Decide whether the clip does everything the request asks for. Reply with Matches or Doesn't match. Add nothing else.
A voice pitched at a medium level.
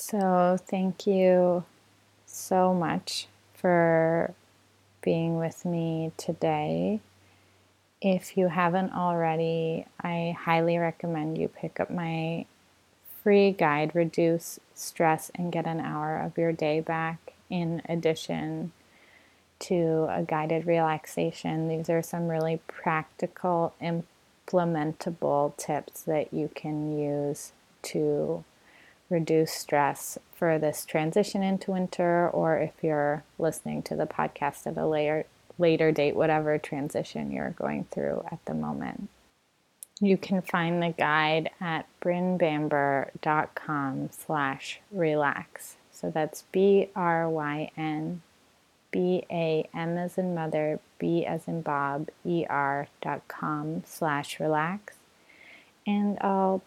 Matches